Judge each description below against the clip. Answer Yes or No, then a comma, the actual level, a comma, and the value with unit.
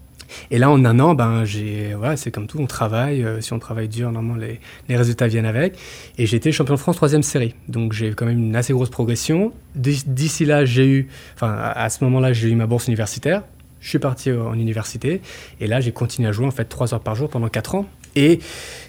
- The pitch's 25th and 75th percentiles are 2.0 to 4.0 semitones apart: Yes, average, 3.7 semitones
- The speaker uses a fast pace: Yes, fast, 240 wpm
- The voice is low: Yes, low, 120 Hz